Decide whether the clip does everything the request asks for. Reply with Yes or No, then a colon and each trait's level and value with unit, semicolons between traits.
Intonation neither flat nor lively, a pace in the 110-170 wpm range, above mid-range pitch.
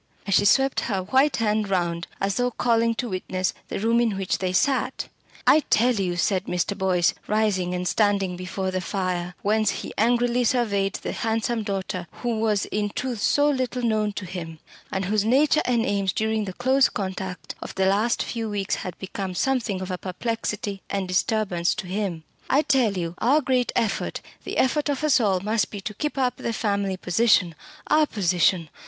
No: average, 4.0 semitones; average, 190 wpm; high, 205 Hz